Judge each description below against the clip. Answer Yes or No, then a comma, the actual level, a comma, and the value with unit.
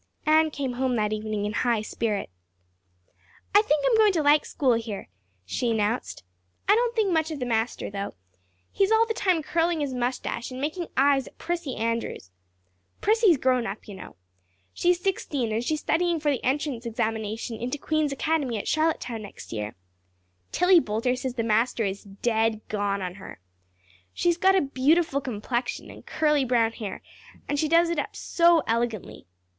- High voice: Yes, very high, 260 Hz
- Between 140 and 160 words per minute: No, average, 175 wpm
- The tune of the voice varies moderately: No, wide, 6.2 semitones